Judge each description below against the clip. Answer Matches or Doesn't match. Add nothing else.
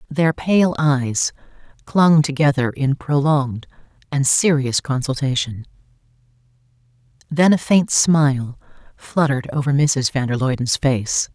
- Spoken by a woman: Matches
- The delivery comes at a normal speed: Doesn't match